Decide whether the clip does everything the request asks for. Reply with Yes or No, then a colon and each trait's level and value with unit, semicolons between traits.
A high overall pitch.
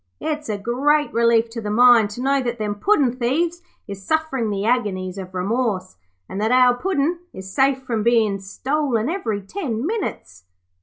Yes: high, 235 Hz